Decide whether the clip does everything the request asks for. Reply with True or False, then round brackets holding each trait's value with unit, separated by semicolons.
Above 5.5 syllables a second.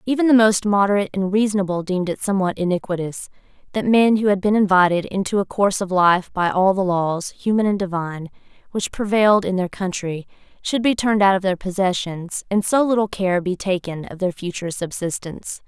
True (5.8 syllables/s)